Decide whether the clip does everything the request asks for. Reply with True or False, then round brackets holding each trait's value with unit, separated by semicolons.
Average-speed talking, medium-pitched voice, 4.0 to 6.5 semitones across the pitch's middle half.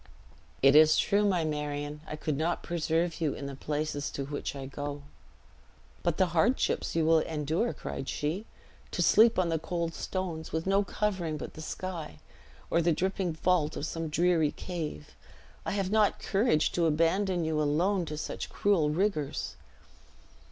False (165 wpm; 165 Hz; 3.4 semitones)